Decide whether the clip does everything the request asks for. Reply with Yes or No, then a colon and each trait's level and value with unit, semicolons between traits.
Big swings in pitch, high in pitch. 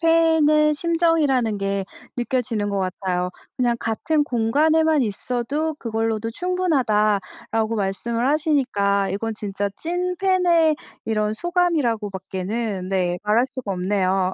Yes: wide, 7.5 semitones; high, 230 Hz